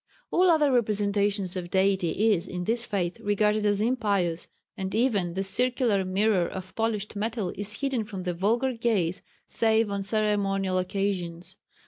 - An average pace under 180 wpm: Yes, average, 150 wpm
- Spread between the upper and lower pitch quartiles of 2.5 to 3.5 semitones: Yes, average, 2.9 semitones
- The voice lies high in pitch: Yes, high, 205 Hz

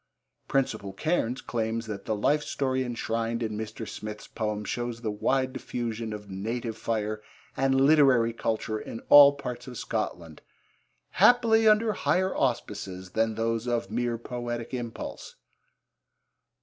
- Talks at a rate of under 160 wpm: Yes, slow, 135 wpm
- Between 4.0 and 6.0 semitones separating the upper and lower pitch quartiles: No, average, 3.1 semitones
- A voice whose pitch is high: No, low, 115 Hz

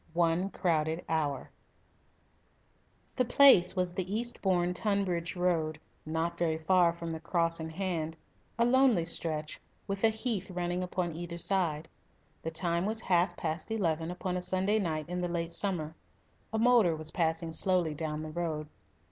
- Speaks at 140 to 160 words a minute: Yes, average, 155 wpm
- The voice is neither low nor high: Yes, medium, 175 Hz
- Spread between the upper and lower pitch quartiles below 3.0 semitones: Yes, narrow, 2.6 semitones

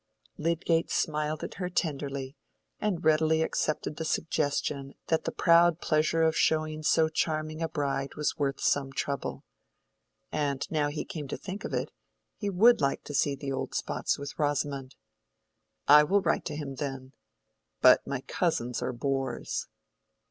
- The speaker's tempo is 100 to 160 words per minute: Yes, average, 155 wpm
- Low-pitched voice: No, medium, 150 Hz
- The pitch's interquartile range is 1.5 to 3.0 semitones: Yes, narrow, 2.5 semitones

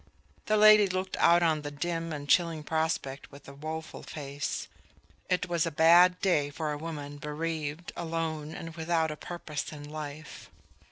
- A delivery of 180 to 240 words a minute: No, average, 165 wpm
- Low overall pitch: No, medium, 160 Hz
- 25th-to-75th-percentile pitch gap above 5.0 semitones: No, narrow, 2.5 semitones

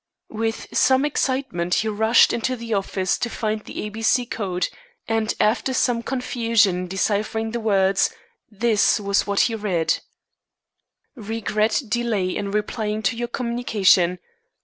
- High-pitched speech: Yes, high, 220 Hz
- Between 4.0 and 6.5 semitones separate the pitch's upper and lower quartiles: No, average, 2.8 semitones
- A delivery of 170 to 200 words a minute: No, average, 145 wpm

